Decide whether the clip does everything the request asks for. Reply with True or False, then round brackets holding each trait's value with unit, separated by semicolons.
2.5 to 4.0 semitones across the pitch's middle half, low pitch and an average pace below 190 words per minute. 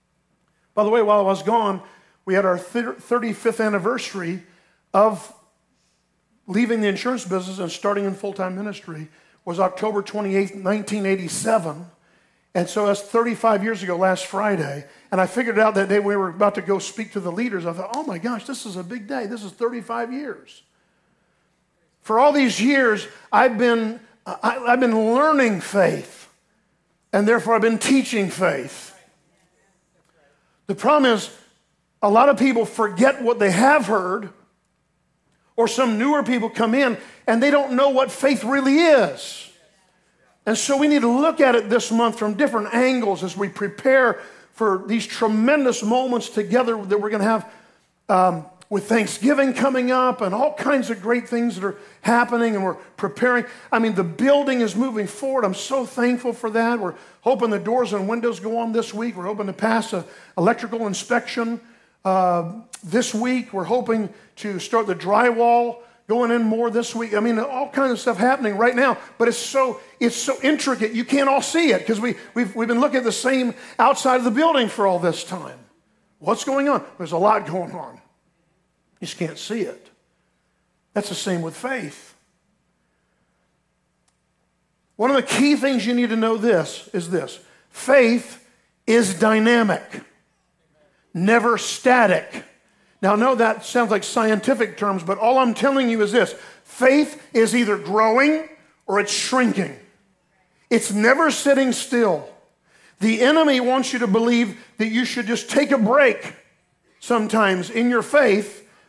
False (3.6 semitones; 225 Hz; 170 wpm)